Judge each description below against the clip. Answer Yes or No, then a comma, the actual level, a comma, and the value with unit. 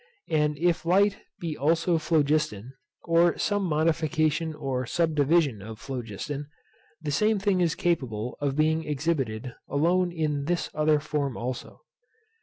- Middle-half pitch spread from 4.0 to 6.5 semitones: No, average, 3.2 semitones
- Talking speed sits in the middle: No, slow, 130 wpm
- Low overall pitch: No, medium, 155 Hz